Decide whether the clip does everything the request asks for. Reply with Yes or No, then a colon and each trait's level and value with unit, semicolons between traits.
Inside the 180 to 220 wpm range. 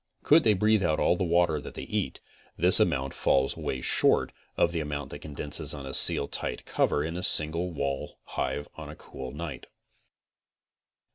Yes: average, 185 wpm